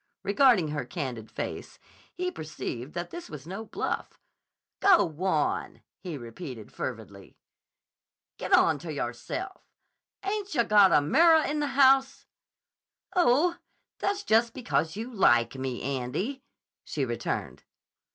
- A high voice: Yes, high, 195 Hz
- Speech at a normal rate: No, slow, 120 wpm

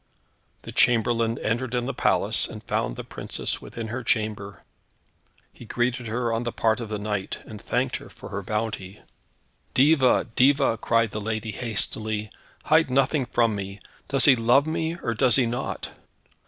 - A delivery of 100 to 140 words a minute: No, average, 170 wpm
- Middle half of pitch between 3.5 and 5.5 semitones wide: No, average, 2.8 semitones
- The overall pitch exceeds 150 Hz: No, low, 115 Hz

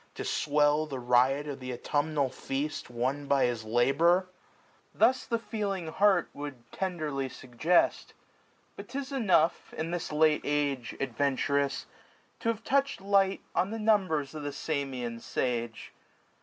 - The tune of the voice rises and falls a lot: Yes, wide, 5.7 semitones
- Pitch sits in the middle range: Yes, medium, 145 Hz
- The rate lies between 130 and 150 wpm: Yes, average, 140 wpm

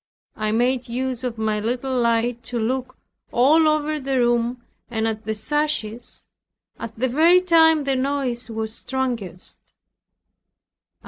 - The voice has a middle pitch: No, high, 245 Hz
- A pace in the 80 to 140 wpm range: Yes, slow, 135 wpm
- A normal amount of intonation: Yes, average, 3.2 semitones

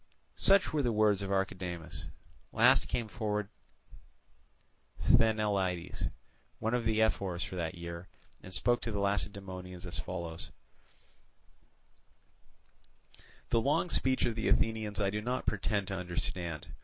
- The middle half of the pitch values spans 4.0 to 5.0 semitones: No, average, 3.5 semitones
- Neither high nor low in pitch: No, low, 100 Hz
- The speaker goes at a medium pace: No, slow, 130 wpm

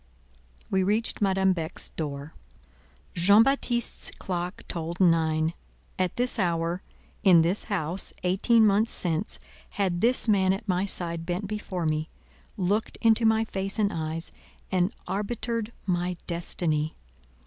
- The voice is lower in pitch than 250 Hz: Yes, medium, 185 Hz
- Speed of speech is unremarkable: No, slow, 130 wpm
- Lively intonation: No, average, 3.8 semitones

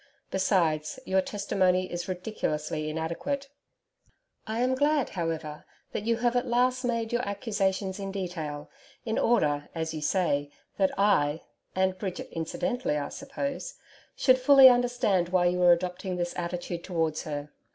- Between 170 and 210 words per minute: No, average, 145 wpm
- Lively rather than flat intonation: Yes, wide, 6.2 semitones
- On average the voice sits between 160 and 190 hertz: Yes, medium, 185 Hz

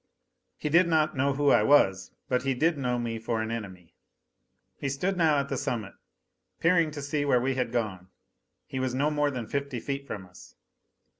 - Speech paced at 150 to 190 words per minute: No, average, 200 wpm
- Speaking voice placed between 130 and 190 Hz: Yes, low, 135 Hz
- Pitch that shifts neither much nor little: Yes, average, 3.9 semitones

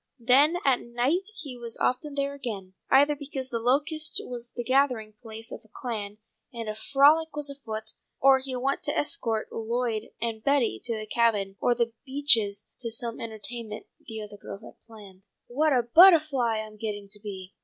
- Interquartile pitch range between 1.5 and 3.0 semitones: No, average, 4.1 semitones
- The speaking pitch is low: No, high, 240 Hz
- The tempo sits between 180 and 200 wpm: Yes, average, 185 wpm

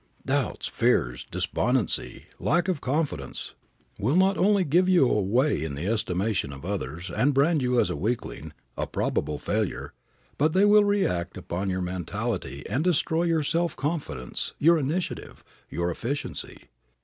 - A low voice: Yes, low, 130 Hz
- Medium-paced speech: Yes, average, 150 wpm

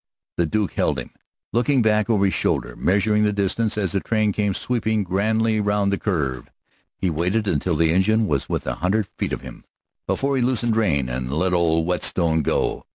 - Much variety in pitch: No, average, 4.4 semitones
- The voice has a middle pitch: No, low, 100 Hz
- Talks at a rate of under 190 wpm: No, average, 195 wpm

